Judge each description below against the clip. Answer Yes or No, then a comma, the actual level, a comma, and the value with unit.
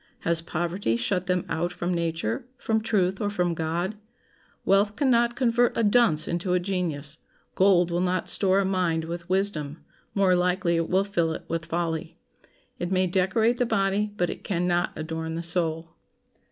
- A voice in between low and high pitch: Yes, medium, 180 Hz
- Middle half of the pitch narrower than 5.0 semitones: Yes, average, 2.8 semitones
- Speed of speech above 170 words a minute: Yes, average, 180 wpm